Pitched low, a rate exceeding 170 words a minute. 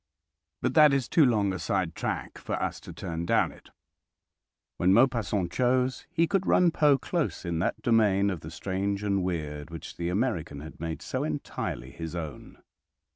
Yes: low, 100 Hz; average, 180 wpm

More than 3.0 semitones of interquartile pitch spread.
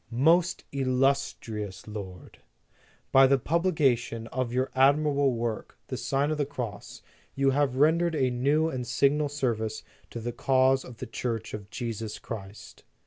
Yes: average, 3.7 semitones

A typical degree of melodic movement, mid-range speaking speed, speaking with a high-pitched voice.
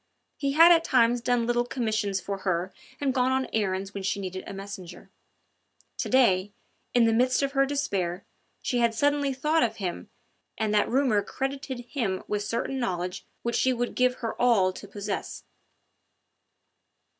Yes: average, 4.9 semitones; average, 165 wpm; high, 235 Hz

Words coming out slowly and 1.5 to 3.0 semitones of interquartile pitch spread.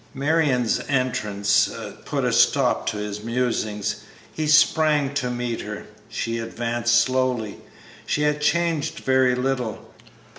No: slow, 120 wpm; average, 3.7 semitones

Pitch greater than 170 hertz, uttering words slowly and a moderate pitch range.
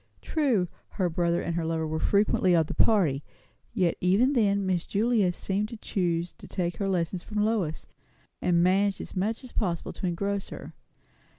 No: medium, 185 Hz; average, 180 wpm; average, 3.4 semitones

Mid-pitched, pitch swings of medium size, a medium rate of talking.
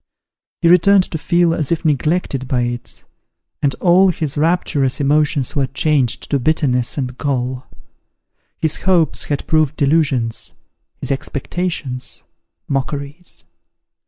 No: medium, 145 Hz; average, 3.9 semitones; slow, 120 wpm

